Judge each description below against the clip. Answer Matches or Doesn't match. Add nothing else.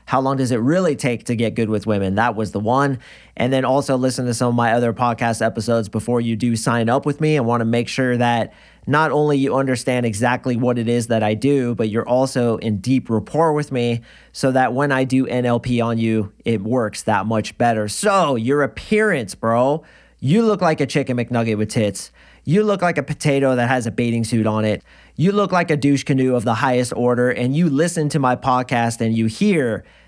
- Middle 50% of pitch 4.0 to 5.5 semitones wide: Doesn't match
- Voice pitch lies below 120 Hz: Doesn't match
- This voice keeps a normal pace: Doesn't match